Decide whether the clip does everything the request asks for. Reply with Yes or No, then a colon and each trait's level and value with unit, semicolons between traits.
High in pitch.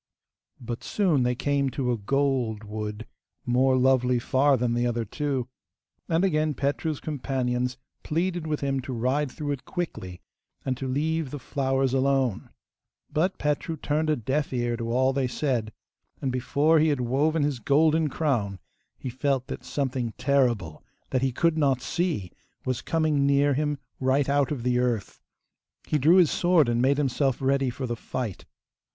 No: low, 135 Hz